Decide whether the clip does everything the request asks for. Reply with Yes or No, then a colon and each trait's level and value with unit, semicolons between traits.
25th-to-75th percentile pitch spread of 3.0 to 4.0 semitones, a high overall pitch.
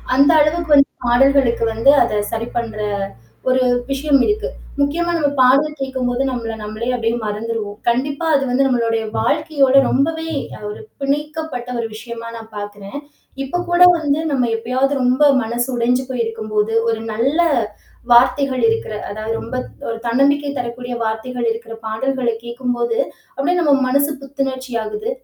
Yes: average, 3.5 semitones; very high, 255 Hz